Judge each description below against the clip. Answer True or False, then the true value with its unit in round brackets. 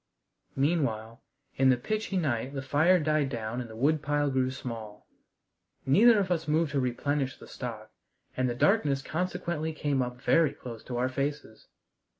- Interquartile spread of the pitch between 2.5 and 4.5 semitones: True (4.1 semitones)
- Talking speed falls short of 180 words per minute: True (160 wpm)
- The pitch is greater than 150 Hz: False (140 Hz)